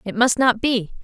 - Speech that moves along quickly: Yes, fast, 230 wpm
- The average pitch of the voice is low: No, high, 230 Hz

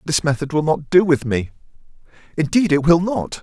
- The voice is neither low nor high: Yes, medium, 155 Hz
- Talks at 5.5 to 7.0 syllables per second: Yes, 5.7 syllables/s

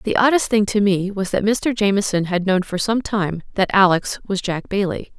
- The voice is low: No, high, 195 Hz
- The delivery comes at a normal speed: No, fast, 220 wpm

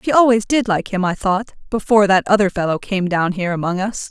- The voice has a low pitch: No, high, 200 Hz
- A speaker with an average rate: No, fast, 235 wpm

